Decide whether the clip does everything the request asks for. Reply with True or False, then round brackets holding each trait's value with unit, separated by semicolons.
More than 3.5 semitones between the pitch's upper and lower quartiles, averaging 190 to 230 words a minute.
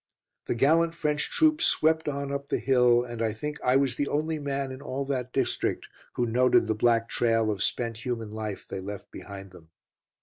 True (4.0 semitones; 200 wpm)